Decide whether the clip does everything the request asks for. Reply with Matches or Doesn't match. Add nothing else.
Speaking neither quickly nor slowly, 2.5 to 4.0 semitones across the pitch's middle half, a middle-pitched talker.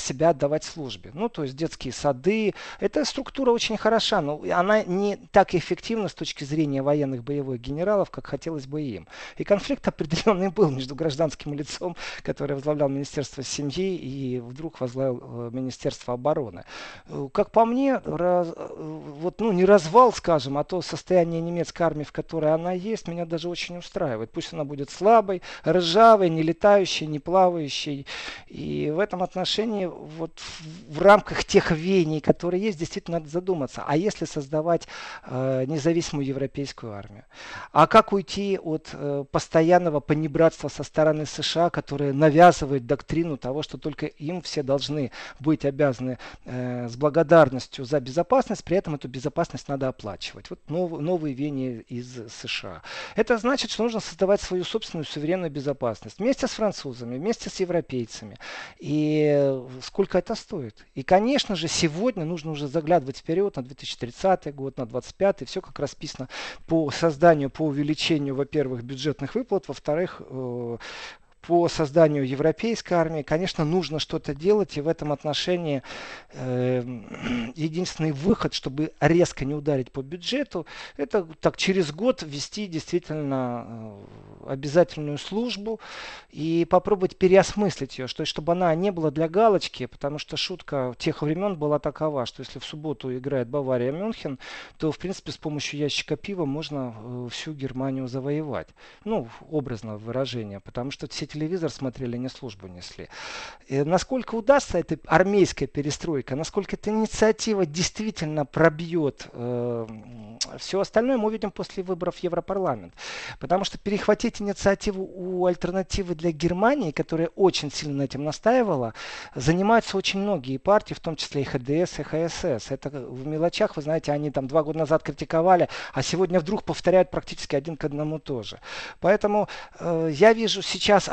Doesn't match